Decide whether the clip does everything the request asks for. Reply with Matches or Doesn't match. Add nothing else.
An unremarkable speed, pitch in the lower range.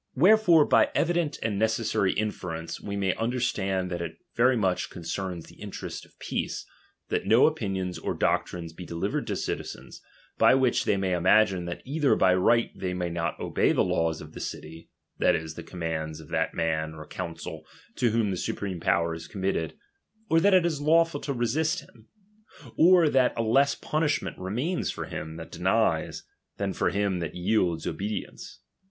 Matches